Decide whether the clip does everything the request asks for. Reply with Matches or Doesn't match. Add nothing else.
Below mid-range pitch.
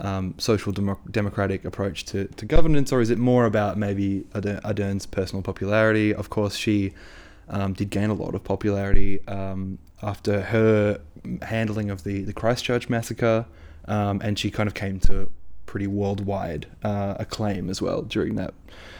Matches